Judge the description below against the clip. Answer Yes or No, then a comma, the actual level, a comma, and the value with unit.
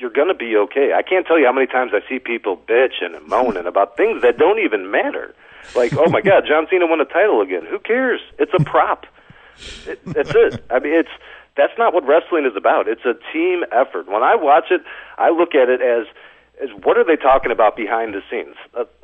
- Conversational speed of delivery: No, fast, 230 wpm